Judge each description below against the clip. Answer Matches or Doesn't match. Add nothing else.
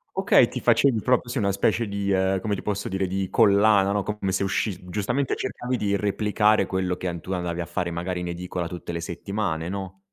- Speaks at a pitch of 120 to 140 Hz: Doesn't match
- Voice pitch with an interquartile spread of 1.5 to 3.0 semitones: Matches